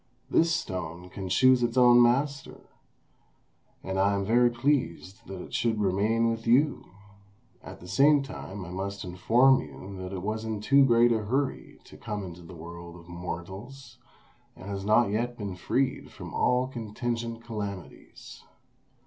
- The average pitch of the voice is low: Yes, low, 110 Hz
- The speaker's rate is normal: Yes, average, 160 wpm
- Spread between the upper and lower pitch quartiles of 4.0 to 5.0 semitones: Yes, average, 4.5 semitones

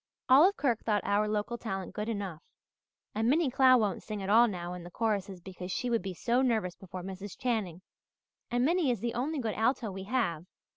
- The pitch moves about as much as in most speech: Yes, average, 4.2 semitones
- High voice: Yes, high, 215 Hz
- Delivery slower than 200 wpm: No, fast, 205 wpm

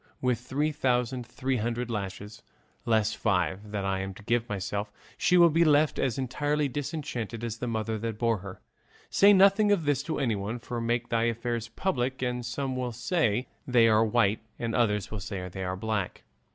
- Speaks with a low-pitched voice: Yes, low, 120 Hz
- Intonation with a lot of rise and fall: No, average, 3.7 semitones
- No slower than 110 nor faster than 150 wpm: No, average, 185 wpm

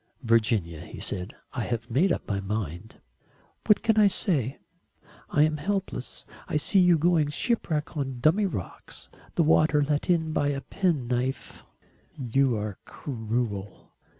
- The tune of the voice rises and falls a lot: Yes, wide, 6.3 semitones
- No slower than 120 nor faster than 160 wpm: Yes, average, 145 wpm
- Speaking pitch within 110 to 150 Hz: Yes, medium, 140 Hz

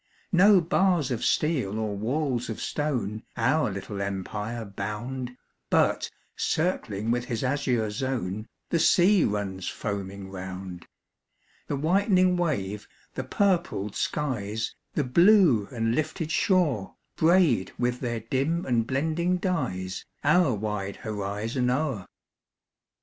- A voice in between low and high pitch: No, low, 125 Hz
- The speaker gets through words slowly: Yes, slow, 115 wpm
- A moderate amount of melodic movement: No, wide, 7.3 semitones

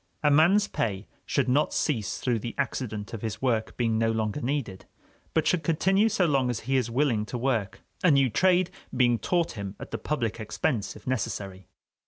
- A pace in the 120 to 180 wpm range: No, average, 195 wpm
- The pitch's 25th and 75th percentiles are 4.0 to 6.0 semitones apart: Yes, average, 5.2 semitones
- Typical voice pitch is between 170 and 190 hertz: No, low, 125 Hz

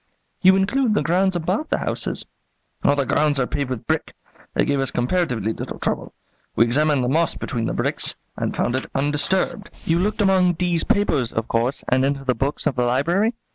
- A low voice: No, medium, 145 Hz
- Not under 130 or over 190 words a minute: No, fast, 205 wpm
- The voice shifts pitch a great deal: Yes, wide, 6.3 semitones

